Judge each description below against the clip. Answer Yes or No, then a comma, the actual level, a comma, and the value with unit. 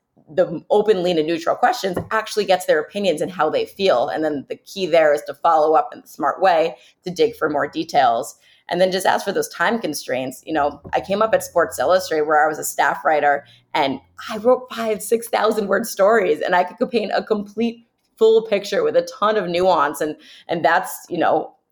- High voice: Yes, high, 200 Hz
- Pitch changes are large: Yes, wide, 5.8 semitones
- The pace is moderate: No, fast, 220 wpm